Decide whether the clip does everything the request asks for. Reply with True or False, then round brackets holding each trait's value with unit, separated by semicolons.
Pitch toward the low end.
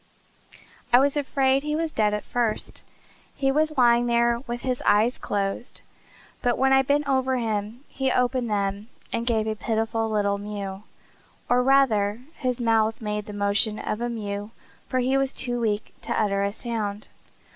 False (235 Hz)